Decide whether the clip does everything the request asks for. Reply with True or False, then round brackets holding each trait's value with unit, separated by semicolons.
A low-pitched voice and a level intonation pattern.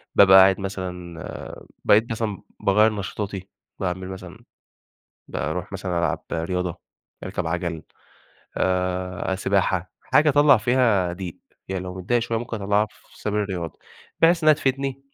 False (95 Hz; 3.3 semitones)